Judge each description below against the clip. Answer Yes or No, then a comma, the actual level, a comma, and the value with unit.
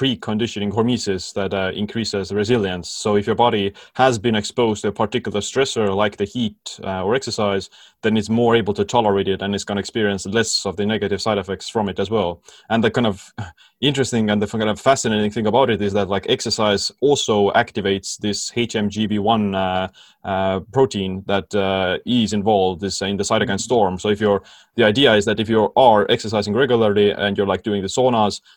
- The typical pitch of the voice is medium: No, low, 105 Hz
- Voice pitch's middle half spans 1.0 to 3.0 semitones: Yes, narrow, 2.5 semitones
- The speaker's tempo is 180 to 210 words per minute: Yes, fast, 205 wpm